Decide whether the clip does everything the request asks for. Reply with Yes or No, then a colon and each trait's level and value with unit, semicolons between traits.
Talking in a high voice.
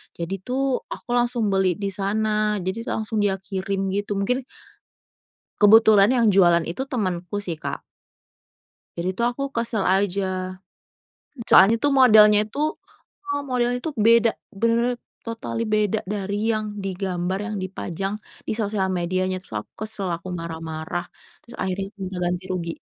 Yes: high, 200 Hz